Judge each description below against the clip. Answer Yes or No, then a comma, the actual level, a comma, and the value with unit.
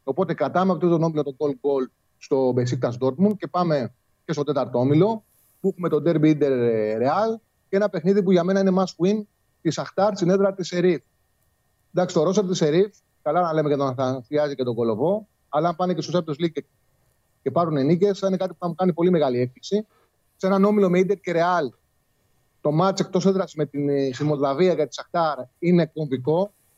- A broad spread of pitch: No, average, 5.0 semitones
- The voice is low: No, medium, 165 Hz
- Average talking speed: No, fast, 205 wpm